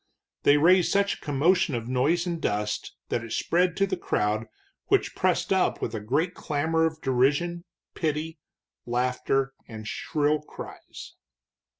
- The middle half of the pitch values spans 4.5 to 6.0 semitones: Yes, wide, 5.5 semitones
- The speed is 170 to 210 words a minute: No, average, 150 wpm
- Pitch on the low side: No, medium, 150 Hz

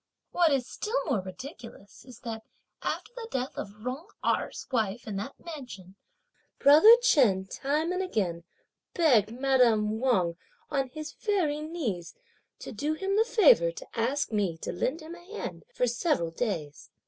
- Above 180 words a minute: No, average, 160 wpm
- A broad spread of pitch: Yes, wide, 7.6 semitones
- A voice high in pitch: Yes, very high, 260 Hz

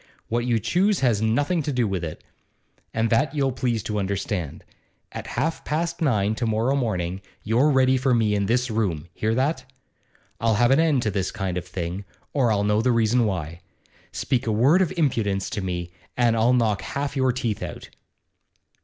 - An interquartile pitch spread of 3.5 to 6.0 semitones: Yes, average, 4.5 semitones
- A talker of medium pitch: No, low, 115 Hz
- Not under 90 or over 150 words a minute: No, average, 190 wpm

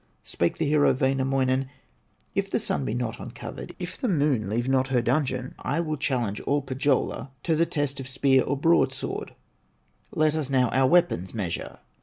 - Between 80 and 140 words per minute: No, average, 175 wpm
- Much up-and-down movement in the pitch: No, narrow, 2.6 semitones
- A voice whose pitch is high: No, low, 135 Hz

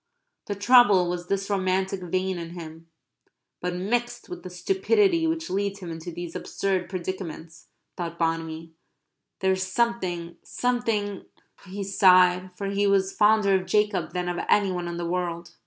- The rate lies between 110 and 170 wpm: Yes, average, 155 wpm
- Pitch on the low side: No, medium, 185 Hz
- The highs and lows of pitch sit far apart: No, narrow, 2.6 semitones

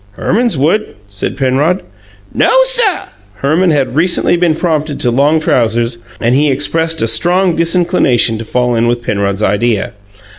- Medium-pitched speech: Yes, medium, 145 Hz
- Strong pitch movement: Yes, wide, 6.3 semitones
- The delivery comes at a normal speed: Yes, average, 150 wpm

